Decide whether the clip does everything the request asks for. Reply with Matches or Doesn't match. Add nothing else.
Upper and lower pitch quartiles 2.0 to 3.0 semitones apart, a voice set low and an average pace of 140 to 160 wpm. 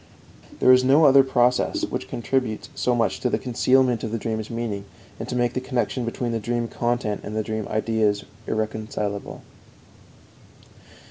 Matches